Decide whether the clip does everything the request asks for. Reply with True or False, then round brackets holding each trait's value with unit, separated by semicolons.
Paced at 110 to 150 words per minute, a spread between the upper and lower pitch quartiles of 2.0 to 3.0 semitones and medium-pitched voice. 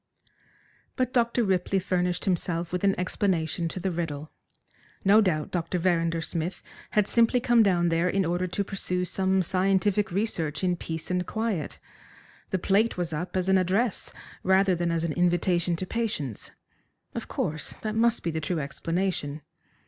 False (165 wpm; 2.7 semitones; 180 Hz)